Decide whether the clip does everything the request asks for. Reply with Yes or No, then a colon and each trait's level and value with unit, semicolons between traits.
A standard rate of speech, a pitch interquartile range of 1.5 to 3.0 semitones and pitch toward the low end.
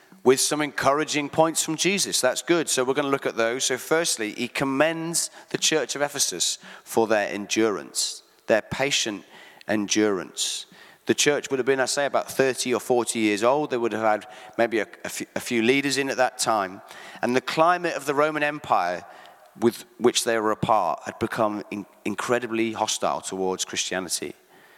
No: average, 180 wpm; average, 4.7 semitones; low, 125 Hz